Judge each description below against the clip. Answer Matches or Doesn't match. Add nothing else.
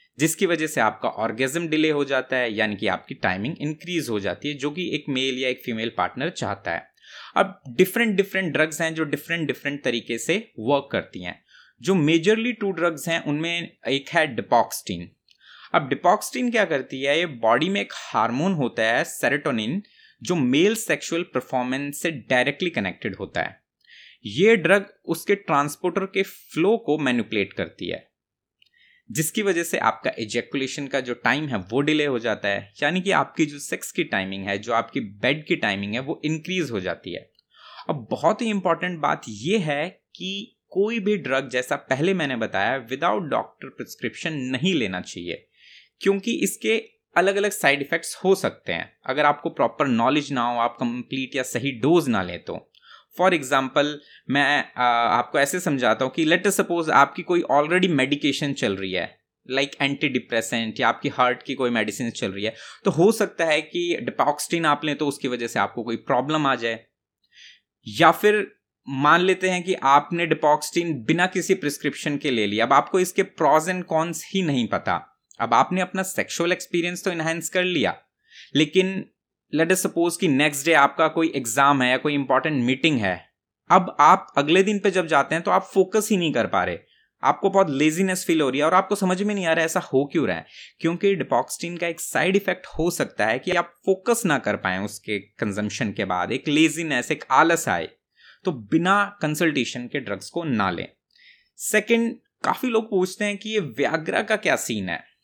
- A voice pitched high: Doesn't match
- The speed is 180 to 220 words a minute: Matches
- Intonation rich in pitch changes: Matches